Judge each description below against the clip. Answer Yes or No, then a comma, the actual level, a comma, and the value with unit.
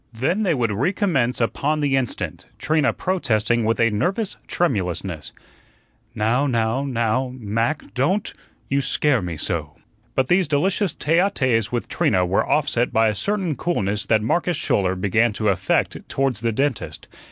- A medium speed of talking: Yes, average, 155 wpm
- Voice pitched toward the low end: Yes, low, 125 Hz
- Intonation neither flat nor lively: No, wide, 5.9 semitones